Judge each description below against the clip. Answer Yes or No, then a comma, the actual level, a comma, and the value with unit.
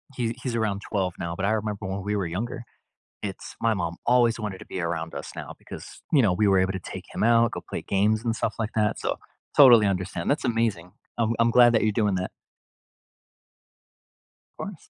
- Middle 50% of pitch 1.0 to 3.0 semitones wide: No, average, 3.5 semitones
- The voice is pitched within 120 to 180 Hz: No, low, 105 Hz